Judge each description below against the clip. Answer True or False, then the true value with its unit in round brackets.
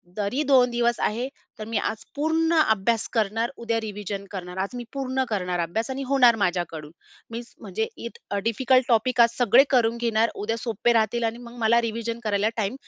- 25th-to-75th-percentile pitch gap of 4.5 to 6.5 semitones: False (2.7 semitones)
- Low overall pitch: False (230 Hz)